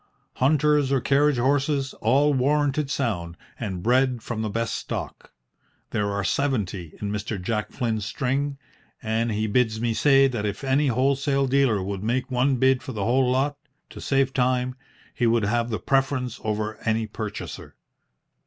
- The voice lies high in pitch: No, low, 125 Hz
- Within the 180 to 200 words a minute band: No, average, 160 wpm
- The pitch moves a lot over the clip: No, average, 3.9 semitones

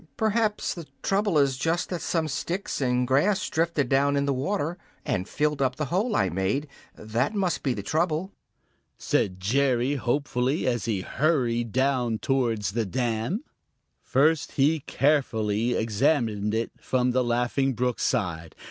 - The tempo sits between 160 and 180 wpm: No, average, 150 wpm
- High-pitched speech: No, low, 135 Hz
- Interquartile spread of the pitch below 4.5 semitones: No, average, 4.8 semitones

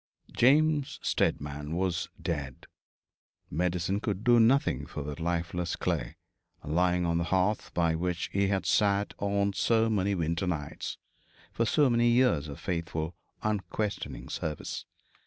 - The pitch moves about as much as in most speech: Yes, average, 4.4 semitones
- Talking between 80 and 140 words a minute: Yes, slow, 135 wpm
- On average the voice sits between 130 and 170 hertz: No, very low, 90 Hz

